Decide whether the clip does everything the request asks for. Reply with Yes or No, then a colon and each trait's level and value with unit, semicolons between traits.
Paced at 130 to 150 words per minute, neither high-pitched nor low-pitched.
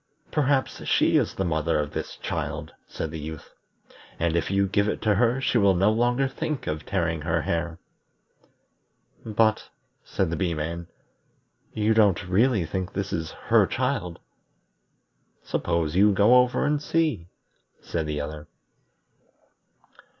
No: average, 145 wpm; very low, 95 Hz